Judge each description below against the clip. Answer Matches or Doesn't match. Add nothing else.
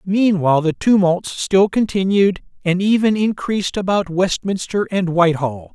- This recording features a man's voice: Matches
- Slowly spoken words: Matches